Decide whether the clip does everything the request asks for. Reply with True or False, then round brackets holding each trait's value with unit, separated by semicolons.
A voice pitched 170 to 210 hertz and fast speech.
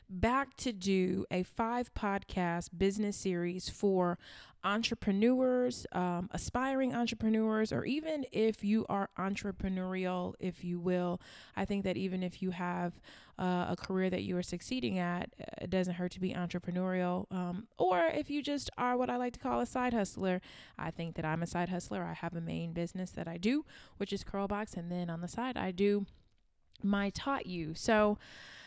False (190 Hz; 180 wpm)